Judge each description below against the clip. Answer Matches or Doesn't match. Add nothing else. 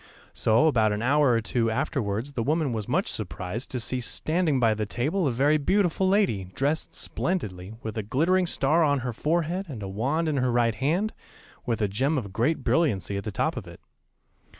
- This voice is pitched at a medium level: Doesn't match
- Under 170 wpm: Doesn't match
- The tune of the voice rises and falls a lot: Matches